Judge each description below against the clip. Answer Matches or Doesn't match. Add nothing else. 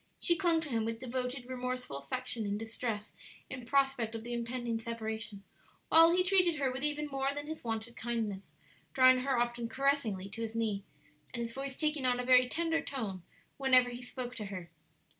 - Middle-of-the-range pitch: Doesn't match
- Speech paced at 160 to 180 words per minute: Doesn't match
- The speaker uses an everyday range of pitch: Matches